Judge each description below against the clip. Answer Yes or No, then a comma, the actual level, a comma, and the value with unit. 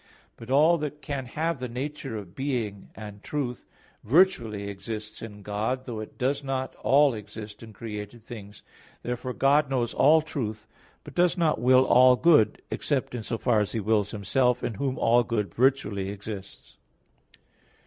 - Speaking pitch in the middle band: No, low, 120 Hz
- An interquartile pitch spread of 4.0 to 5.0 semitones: Yes, average, 4.3 semitones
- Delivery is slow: No, average, 165 wpm